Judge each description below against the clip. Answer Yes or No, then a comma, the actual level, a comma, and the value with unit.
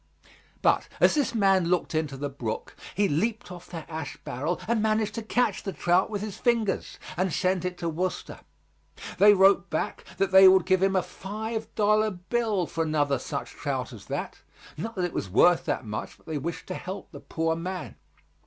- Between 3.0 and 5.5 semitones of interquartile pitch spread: Yes, average, 4.2 semitones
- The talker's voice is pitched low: No, medium, 185 Hz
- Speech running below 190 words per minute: No, average, 200 wpm